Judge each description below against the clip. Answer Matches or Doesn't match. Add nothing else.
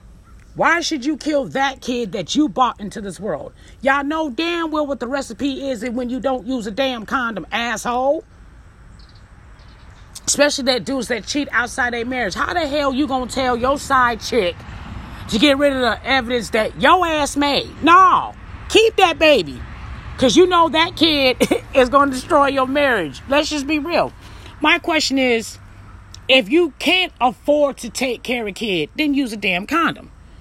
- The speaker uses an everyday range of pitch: Matches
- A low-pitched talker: Doesn't match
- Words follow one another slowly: Doesn't match